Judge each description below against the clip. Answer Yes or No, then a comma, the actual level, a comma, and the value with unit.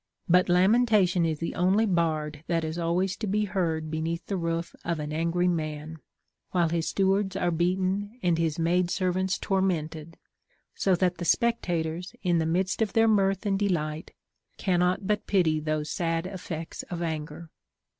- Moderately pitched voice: Yes, medium, 175 Hz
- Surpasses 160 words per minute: Yes, average, 170 wpm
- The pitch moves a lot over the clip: No, average, 2.7 semitones